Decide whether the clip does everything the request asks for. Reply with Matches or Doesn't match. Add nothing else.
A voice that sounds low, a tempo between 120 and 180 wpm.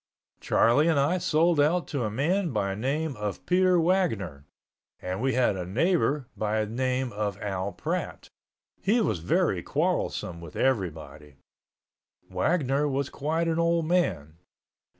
Matches